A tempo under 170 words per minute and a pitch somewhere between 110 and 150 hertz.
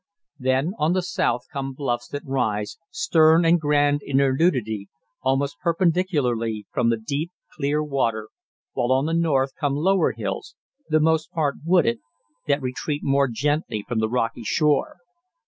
Yes: average, 155 wpm; medium, 140 Hz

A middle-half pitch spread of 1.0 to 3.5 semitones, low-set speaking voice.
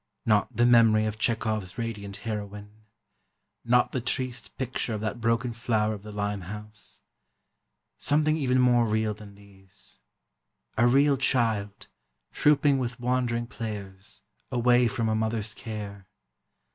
Yes: average, 2.7 semitones; low, 110 Hz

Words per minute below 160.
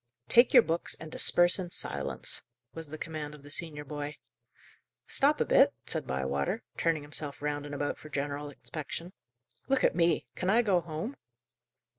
No: average, 170 wpm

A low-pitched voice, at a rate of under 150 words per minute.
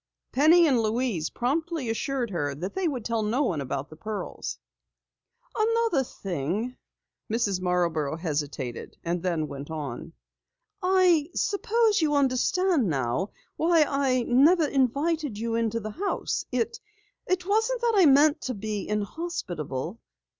No: high, 240 Hz; slow, 135 wpm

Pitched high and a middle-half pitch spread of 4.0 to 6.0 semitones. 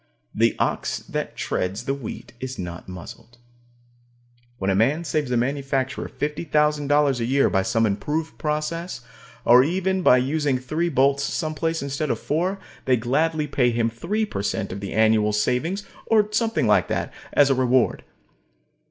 No: medium, 140 Hz; average, 4.7 semitones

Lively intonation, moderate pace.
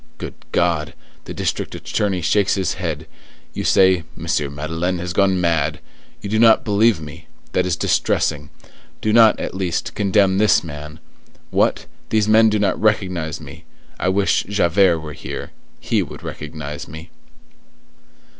No: average, 4.2 semitones; average, 150 wpm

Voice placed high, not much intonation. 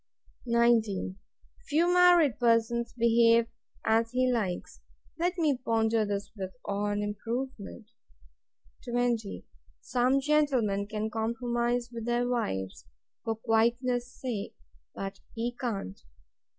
Yes: high, 235 Hz; narrow, 2.3 semitones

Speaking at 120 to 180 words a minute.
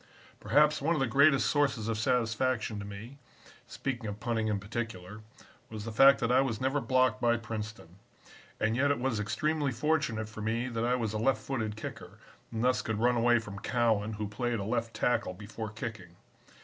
No: average, 195 wpm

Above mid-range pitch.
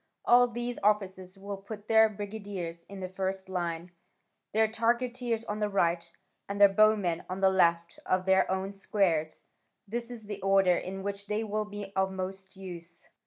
Yes: high, 195 Hz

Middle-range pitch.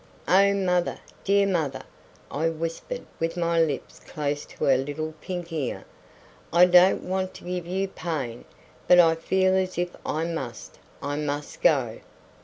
Yes: medium, 170 Hz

